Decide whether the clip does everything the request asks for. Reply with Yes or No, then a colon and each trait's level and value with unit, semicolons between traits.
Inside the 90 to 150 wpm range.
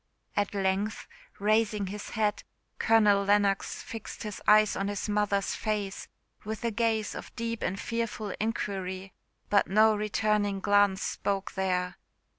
Yes: slow, 135 wpm